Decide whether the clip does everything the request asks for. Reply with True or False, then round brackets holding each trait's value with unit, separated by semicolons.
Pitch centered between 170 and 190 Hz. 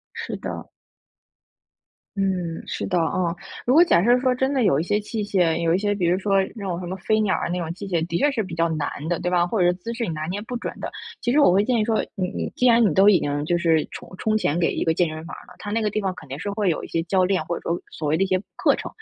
True (185 Hz)